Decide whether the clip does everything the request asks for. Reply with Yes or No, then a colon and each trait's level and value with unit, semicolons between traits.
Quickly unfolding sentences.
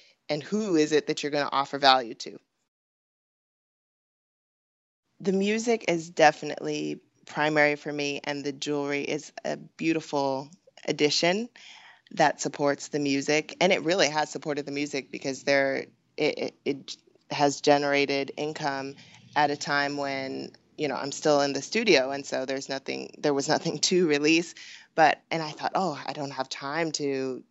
No: average, 160 wpm